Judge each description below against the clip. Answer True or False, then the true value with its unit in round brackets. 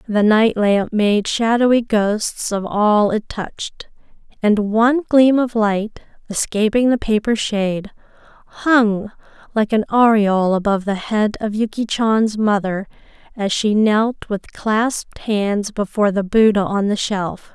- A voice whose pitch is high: True (215 Hz)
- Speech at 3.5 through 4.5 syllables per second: True (4.0 syllables/s)